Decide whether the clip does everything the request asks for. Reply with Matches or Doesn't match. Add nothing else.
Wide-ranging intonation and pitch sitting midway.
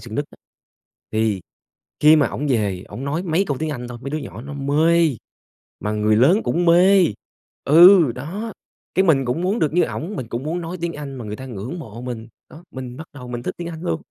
Matches